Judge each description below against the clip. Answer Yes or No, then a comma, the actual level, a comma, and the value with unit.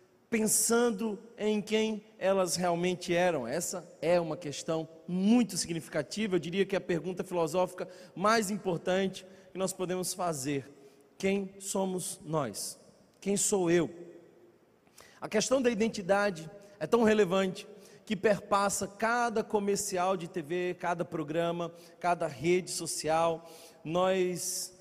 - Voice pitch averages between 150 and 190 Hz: Yes, medium, 185 Hz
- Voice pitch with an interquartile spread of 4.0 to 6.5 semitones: No, average, 2.8 semitones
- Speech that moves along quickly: No, slow, 120 wpm